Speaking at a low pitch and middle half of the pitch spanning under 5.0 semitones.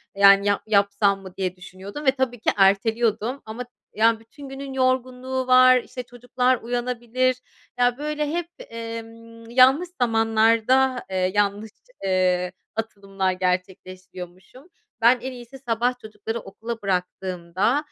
No: high, 225 Hz; average, 4.3 semitones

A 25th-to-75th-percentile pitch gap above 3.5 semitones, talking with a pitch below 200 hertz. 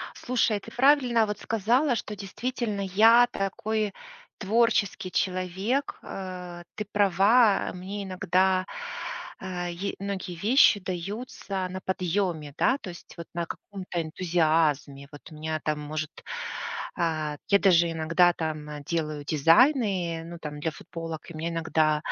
Yes: average, 4.0 semitones; medium, 185 Hz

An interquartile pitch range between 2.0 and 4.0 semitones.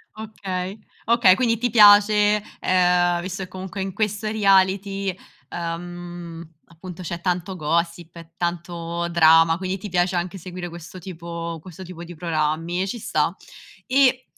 Yes: narrow, 2.5 semitones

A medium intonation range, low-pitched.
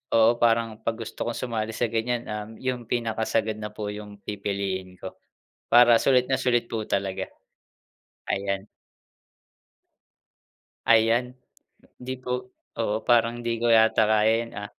No: narrow, 2.1 semitones; low, 115 Hz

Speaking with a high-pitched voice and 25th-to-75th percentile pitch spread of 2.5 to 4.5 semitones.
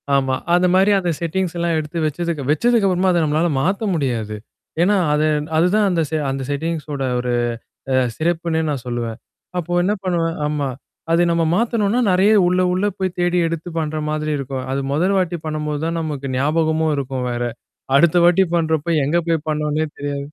No: medium, 160 Hz; average, 3.3 semitones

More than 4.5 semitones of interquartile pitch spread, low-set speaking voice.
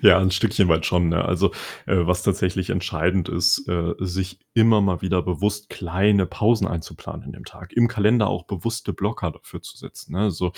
No: average, 2.8 semitones; very low, 95 Hz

